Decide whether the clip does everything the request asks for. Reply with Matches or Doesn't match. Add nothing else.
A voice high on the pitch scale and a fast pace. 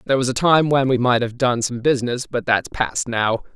Doesn't match